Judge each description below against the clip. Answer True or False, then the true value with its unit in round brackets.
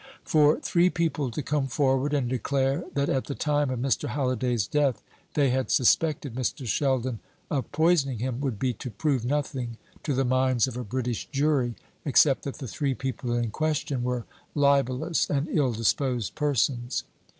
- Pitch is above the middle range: False (135 Hz)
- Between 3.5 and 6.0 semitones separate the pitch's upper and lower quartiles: False (2.8 semitones)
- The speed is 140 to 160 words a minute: False (170 wpm)